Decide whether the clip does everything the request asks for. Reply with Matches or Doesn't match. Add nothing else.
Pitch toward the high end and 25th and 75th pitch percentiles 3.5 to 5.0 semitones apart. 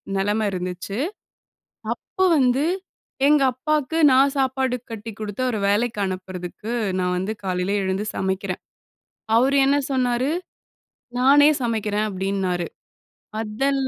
Doesn't match